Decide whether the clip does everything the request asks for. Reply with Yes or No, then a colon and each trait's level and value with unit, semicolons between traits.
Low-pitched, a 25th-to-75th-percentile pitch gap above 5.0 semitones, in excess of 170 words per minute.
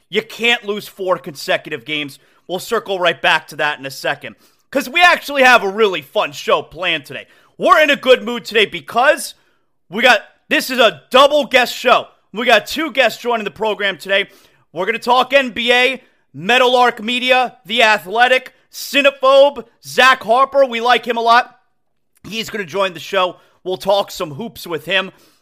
No: high, 225 Hz; wide, 5.6 semitones; average, 180 wpm